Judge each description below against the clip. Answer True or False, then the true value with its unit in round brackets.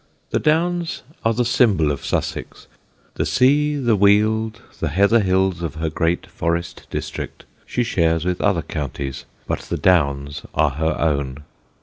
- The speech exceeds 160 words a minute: False (150 wpm)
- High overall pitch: False (90 Hz)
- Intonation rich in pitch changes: True (6.3 semitones)